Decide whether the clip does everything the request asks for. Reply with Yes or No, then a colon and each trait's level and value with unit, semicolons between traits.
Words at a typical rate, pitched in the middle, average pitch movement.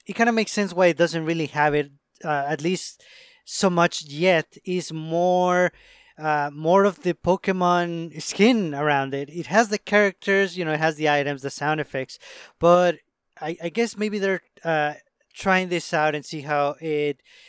Yes: average, 185 wpm; medium, 170 Hz; average, 3.8 semitones